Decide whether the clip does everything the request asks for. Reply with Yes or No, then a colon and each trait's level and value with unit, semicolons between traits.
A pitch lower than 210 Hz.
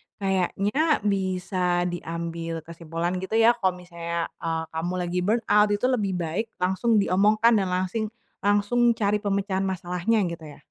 Yes: high, 190 Hz